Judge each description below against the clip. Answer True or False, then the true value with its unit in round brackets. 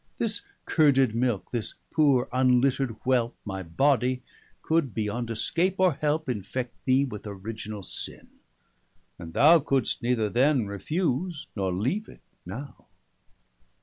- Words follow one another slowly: True (130 wpm)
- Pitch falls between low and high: False (125 Hz)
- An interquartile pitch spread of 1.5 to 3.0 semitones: False (5.1 semitones)